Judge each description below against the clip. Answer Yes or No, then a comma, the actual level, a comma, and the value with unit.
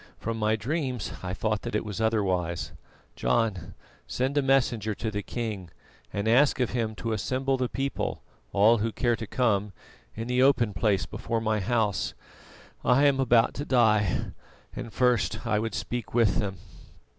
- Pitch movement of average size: Yes, average, 3.1 semitones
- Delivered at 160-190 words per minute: Yes, average, 170 wpm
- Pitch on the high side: No, low, 115 Hz